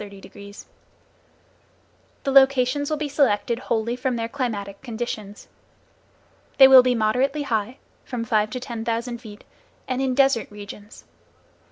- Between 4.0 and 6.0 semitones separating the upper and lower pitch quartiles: No, average, 3.6 semitones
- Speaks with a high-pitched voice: Yes, high, 240 Hz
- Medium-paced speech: No, slow, 130 wpm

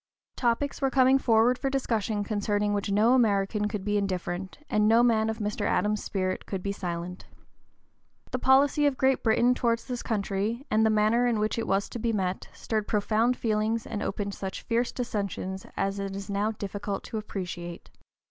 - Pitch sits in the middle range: No, high, 215 Hz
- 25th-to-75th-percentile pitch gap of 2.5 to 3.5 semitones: Yes, average, 2.8 semitones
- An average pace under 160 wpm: No, average, 185 wpm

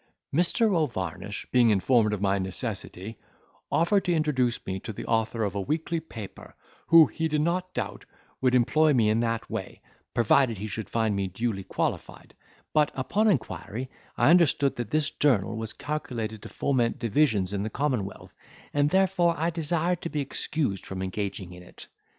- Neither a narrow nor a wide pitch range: No, wide, 6.9 semitones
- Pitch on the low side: Yes, low, 120 Hz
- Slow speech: No, average, 170 wpm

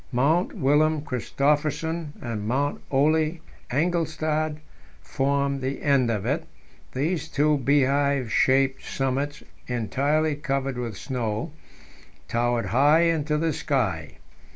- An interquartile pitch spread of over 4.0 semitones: No, average, 3.1 semitones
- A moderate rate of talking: No, slow, 105 wpm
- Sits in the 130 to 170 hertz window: Yes, medium, 140 Hz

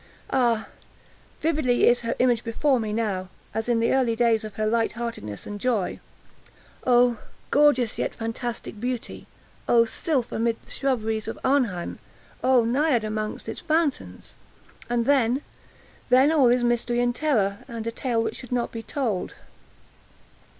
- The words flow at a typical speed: Yes, average, 150 wpm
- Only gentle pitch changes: Yes, narrow, 2.3 semitones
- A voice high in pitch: Yes, high, 235 Hz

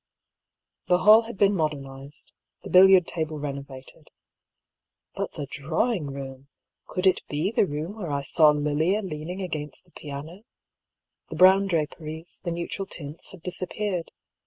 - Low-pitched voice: No, medium, 160 Hz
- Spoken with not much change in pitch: No, average, 4.2 semitones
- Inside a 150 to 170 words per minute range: No, average, 140 wpm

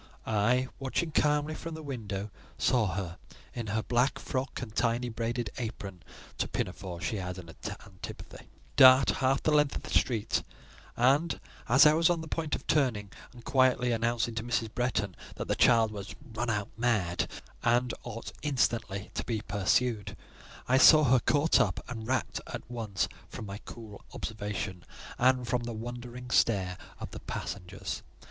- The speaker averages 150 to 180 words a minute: Yes, average, 160 wpm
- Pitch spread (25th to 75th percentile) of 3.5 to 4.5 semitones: Yes, average, 3.8 semitones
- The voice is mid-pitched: No, low, 120 Hz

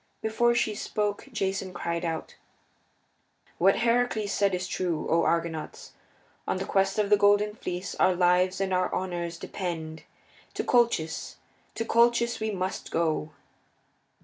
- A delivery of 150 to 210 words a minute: No, average, 140 wpm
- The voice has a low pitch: No, high, 190 Hz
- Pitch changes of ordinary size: Yes, average, 3.6 semitones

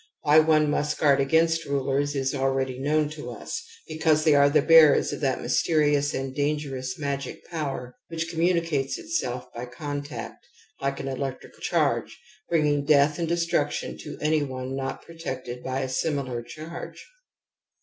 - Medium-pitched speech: Yes, medium, 145 Hz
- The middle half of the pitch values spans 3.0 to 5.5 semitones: No, narrow, 2.6 semitones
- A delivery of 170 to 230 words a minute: No, average, 155 wpm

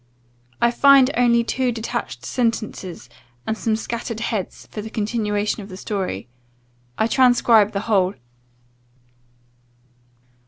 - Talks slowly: Yes, slow, 115 wpm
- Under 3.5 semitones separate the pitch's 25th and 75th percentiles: Yes, narrow, 2.4 semitones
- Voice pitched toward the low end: No, high, 220 Hz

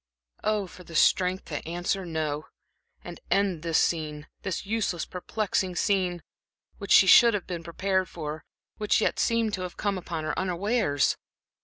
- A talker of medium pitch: Yes, medium, 180 Hz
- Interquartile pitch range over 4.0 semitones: No, average, 3.3 semitones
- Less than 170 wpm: Yes, average, 160 wpm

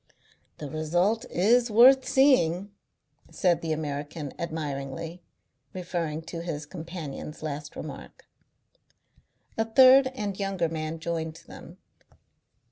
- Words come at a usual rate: No, slow, 105 wpm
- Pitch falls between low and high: Yes, medium, 170 Hz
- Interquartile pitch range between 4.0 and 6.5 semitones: Yes, average, 4.5 semitones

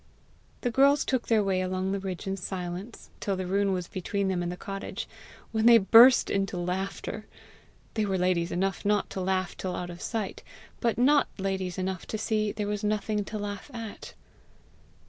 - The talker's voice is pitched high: Yes, high, 195 Hz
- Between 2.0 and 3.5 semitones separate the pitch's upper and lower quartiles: Yes, narrow, 2.5 semitones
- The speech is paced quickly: No, average, 185 wpm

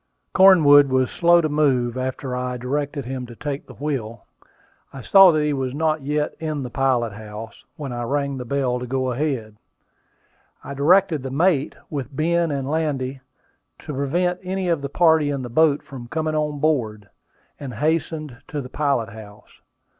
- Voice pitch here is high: No, medium, 140 Hz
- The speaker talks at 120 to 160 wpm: No, average, 175 wpm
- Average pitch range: Yes, average, 3.4 semitones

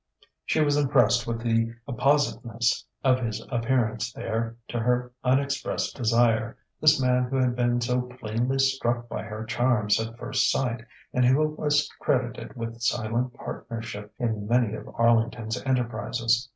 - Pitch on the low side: Yes, low, 120 Hz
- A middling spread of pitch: No, narrow, 1.9 semitones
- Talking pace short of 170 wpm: Yes, average, 145 wpm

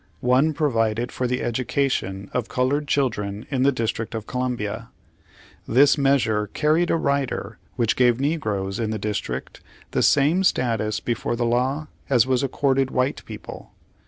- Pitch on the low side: Yes, low, 125 Hz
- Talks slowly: No, average, 150 wpm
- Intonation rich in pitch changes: No, average, 3.9 semitones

